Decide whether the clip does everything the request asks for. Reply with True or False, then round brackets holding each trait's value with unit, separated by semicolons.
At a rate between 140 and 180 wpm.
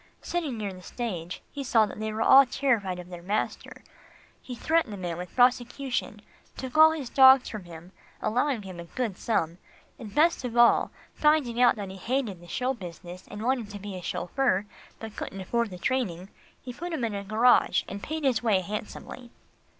False (195 wpm)